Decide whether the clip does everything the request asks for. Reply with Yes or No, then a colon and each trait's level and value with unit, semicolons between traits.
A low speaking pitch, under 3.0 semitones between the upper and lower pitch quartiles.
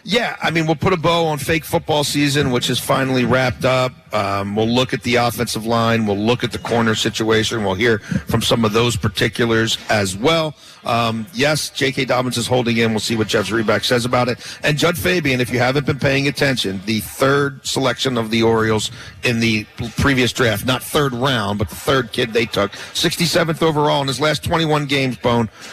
No: low, 125 Hz; average, 3.9 semitones